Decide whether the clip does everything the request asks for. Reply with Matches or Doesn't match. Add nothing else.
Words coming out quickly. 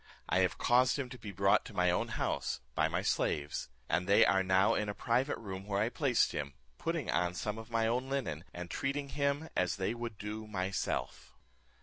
Matches